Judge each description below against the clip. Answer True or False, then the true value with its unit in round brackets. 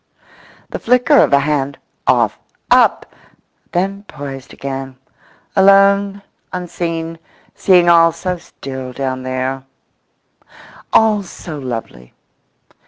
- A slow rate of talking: True (95 wpm)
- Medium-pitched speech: True (165 Hz)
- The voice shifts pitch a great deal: True (6.3 semitones)